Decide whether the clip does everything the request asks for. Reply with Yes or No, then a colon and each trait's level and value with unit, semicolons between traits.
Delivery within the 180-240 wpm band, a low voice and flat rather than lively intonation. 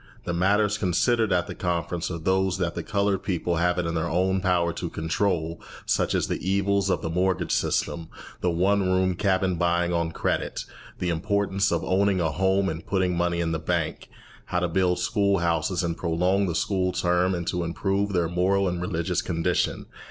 Yes: average, 195 wpm; very low, 90 Hz; narrow, 2.0 semitones